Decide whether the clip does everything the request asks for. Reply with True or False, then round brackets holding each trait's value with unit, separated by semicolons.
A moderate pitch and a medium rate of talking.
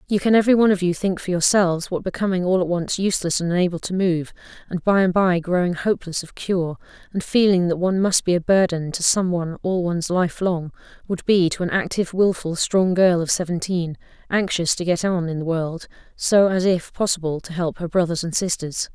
False (180 Hz; 220 wpm)